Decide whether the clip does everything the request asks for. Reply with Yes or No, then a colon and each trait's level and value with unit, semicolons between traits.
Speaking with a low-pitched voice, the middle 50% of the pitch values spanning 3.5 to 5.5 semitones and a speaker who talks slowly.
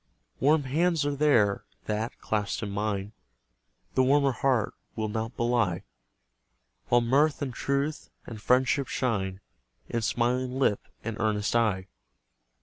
Yes: low, 120 Hz; average, 4.3 semitones; slow, 130 wpm